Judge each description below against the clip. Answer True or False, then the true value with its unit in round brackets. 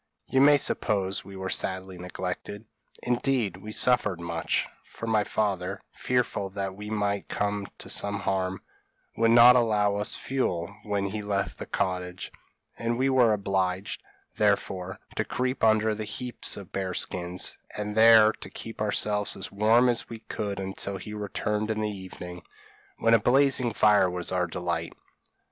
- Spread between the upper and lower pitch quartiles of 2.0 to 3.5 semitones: True (2.9 semitones)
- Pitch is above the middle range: False (105 Hz)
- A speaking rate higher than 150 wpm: True (160 wpm)